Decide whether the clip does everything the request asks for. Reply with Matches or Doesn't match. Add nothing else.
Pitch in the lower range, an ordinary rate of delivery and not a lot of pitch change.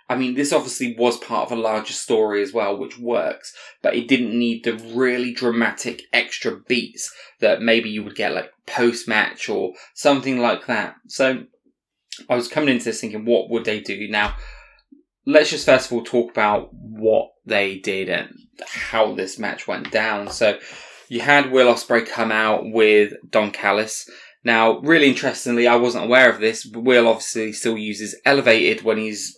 Matches